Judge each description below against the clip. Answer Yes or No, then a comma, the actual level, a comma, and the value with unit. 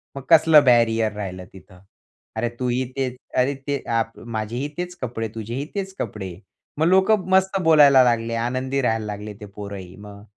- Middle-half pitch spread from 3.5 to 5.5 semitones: Yes, average, 4.9 semitones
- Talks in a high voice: No, low, 120 Hz